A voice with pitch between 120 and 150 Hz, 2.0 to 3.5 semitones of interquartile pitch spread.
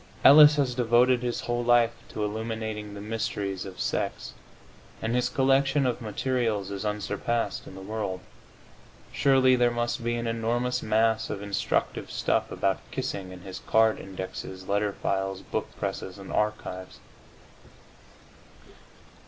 No: low, 110 Hz; average, 3.2 semitones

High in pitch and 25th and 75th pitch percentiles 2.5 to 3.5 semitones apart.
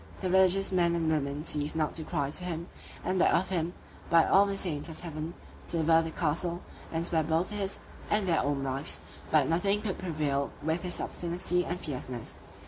No: medium, 165 Hz; average, 2.8 semitones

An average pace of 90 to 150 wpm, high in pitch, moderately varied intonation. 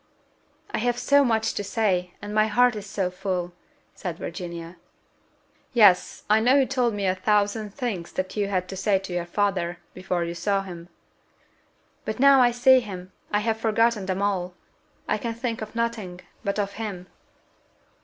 No: average, 180 wpm; high, 205 Hz; average, 3.7 semitones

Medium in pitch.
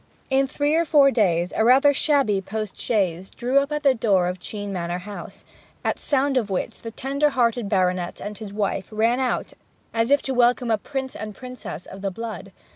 No: high, 225 Hz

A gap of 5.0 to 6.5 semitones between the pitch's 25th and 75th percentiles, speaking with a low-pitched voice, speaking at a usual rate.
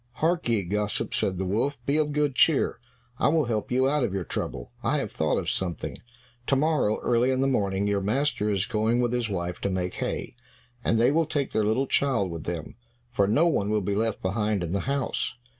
No: wide, 5.5 semitones; low, 110 Hz; fast, 225 wpm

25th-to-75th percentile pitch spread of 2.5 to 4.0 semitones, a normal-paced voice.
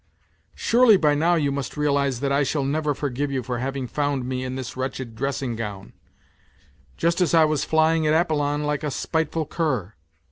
Yes: average, 3.1 semitones; average, 185 wpm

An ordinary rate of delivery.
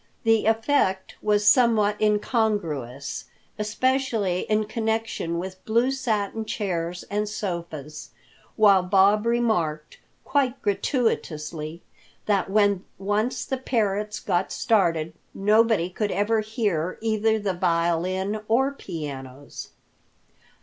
No: slow, 100 wpm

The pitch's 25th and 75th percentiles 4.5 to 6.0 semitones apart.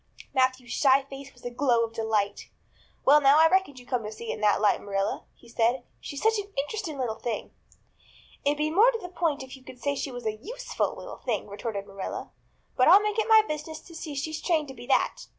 Yes: wide, 5.4 semitones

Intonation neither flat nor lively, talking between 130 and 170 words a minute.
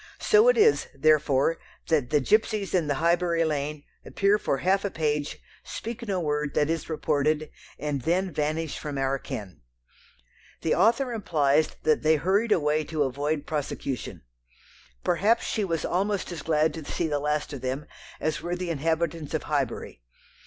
Yes: average, 3.5 semitones; average, 165 wpm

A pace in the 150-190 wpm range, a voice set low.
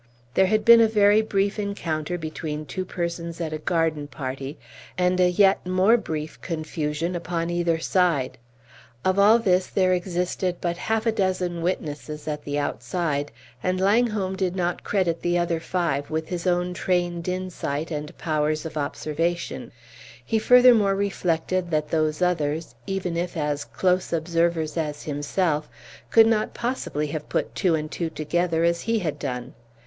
No: average, 160 wpm; medium, 175 Hz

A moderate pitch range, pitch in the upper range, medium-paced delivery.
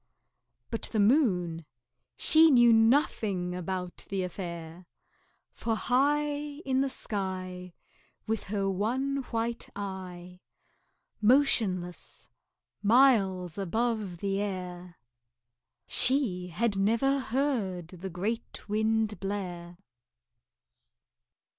No: average, 4.8 semitones; high, 205 Hz; slow, 90 wpm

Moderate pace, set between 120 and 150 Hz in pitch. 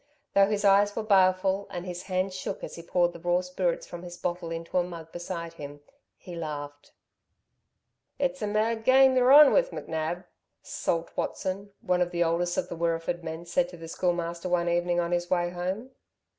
No: average, 195 wpm; medium, 175 Hz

